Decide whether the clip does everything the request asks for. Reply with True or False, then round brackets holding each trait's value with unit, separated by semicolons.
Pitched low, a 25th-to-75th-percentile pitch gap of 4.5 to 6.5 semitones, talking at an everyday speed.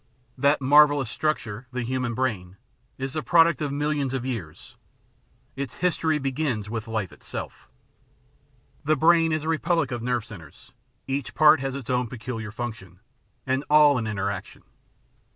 True (130 Hz; 4.9 semitones; 155 wpm)